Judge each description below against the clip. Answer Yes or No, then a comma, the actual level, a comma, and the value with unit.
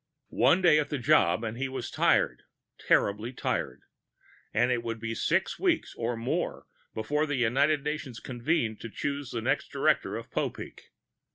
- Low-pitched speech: Yes, low, 125 Hz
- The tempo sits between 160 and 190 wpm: Yes, average, 165 wpm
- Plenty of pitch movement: No, average, 4.5 semitones